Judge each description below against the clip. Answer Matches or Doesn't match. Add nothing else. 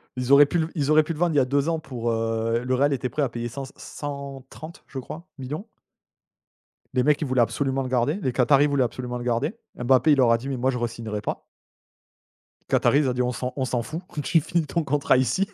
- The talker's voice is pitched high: Doesn't match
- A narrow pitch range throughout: Doesn't match